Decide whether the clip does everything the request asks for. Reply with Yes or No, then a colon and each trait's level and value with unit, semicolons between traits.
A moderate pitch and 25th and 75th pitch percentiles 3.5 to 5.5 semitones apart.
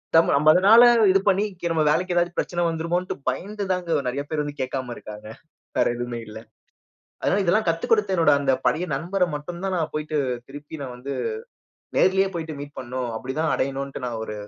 Yes: medium, 155 Hz; average, 5.0 semitones